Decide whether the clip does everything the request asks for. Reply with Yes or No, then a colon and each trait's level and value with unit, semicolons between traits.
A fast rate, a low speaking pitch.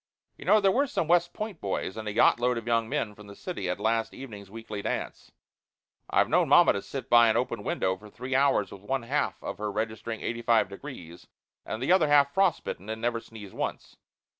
Yes: fast, 215 wpm; low, 115 Hz